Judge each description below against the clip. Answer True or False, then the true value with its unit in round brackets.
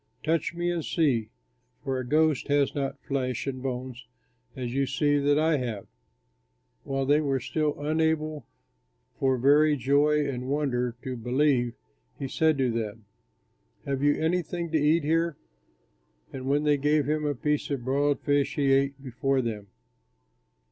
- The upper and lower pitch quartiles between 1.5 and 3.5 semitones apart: True (2.6 semitones)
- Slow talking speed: False (155 wpm)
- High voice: False (140 Hz)